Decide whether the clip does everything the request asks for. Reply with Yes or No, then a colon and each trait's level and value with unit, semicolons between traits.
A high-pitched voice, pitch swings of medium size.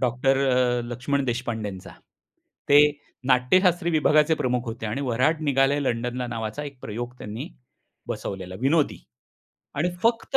No: low, 130 Hz; average, 3.7 semitones